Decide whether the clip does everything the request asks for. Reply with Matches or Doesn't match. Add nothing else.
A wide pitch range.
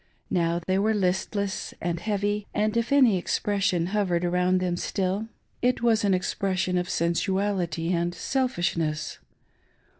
Doesn't match